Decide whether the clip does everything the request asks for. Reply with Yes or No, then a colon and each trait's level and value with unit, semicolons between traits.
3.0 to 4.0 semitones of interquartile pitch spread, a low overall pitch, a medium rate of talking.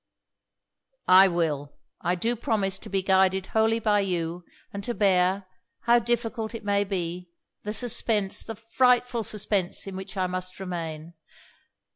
No: average, 3.5 semitones; high, 195 Hz; average, 145 wpm